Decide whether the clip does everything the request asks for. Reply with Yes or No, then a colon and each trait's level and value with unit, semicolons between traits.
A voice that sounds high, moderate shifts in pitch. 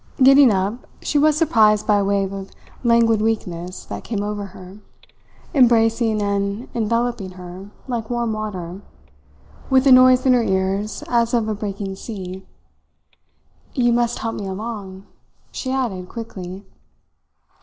Yes: high, 215 Hz; average, 3.4 semitones